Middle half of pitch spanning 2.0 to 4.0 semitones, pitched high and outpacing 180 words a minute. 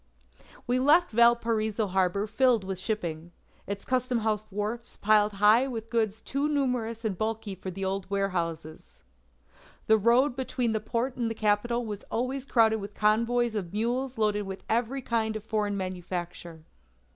No: average, 3.1 semitones; high, 220 Hz; average, 155 wpm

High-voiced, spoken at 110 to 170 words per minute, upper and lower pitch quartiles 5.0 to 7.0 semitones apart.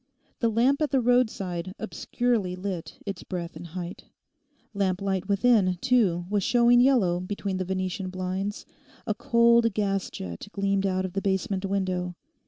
No: high, 195 Hz; average, 155 wpm; average, 3.7 semitones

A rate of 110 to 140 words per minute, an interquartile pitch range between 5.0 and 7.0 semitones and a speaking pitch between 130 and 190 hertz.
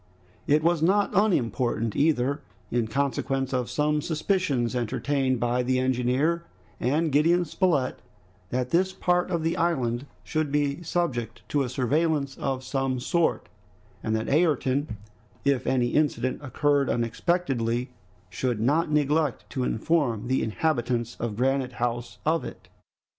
No: slow, 135 wpm; average, 4.3 semitones; low, 135 Hz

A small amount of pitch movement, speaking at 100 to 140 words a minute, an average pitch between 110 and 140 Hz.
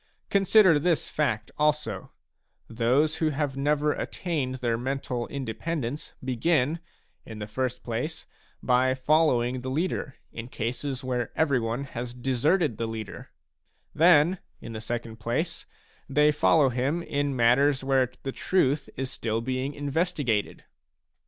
No: average, 4.0 semitones; slow, 135 wpm; low, 135 Hz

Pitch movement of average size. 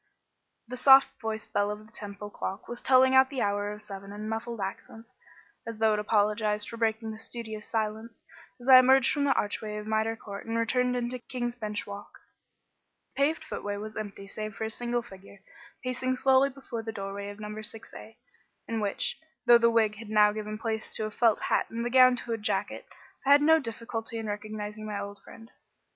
No: narrow, 2.3 semitones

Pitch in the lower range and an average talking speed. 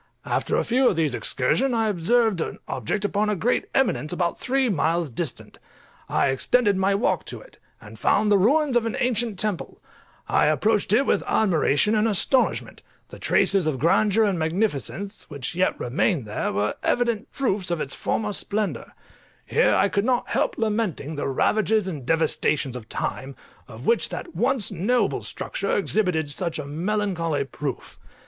No: high, 200 Hz; average, 165 wpm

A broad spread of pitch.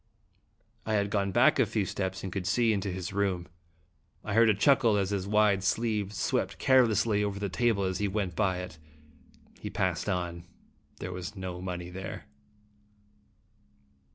No: narrow, 2.5 semitones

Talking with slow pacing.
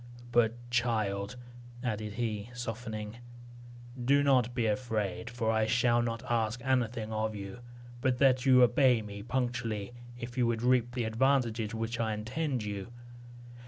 No: average, 145 wpm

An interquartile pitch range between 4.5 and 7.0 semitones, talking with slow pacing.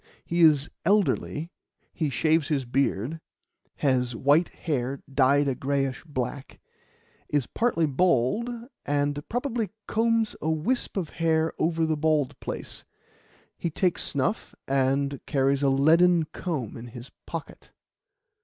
No: average, 3.5 semitones; slow, 125 wpm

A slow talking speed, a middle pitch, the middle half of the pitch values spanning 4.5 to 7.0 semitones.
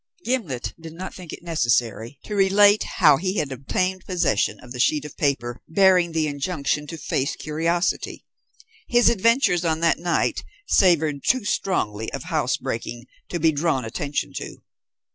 No: average, 160 wpm; medium, 160 Hz; average, 4.9 semitones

